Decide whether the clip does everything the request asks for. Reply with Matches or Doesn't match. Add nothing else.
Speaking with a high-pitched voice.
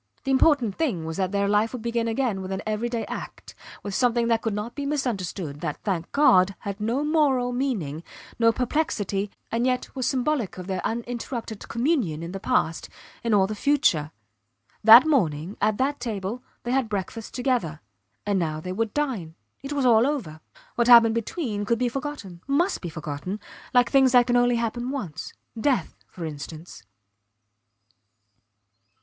Matches